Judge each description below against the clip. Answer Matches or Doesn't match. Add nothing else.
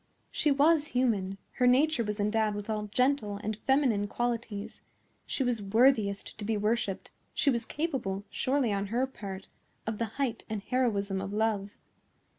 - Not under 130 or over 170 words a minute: Matches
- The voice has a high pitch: Matches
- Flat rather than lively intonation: Doesn't match